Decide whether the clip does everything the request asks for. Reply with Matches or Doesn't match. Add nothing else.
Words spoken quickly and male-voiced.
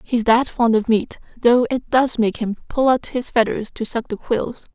Doesn't match